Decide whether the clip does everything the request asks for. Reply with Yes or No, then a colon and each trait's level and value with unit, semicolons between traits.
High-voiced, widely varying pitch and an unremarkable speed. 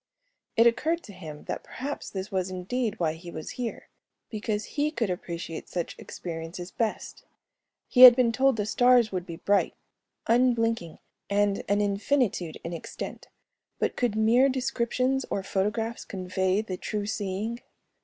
No: high, 210 Hz; average, 4.6 semitones; average, 150 wpm